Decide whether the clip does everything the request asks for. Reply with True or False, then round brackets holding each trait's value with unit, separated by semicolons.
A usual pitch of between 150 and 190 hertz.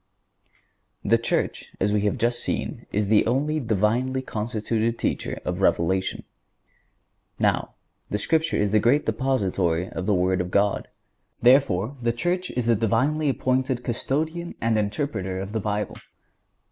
False (115 Hz)